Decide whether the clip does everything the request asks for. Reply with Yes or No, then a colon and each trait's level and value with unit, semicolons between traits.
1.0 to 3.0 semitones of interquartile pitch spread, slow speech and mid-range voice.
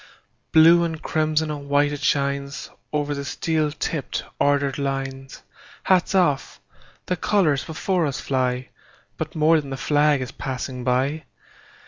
Yes: narrow, 2.5 semitones; slow, 120 wpm; medium, 145 Hz